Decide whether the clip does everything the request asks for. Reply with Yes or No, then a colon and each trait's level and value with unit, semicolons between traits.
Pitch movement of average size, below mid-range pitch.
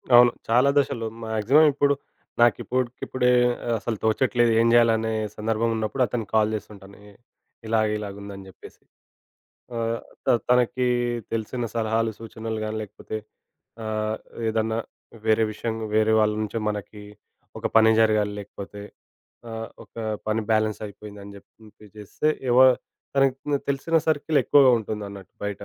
No: narrow, 2.0 semitones; low, 110 Hz